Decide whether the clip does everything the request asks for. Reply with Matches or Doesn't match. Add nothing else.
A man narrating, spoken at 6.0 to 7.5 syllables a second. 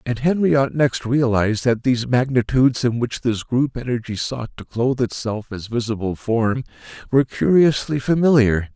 Doesn't match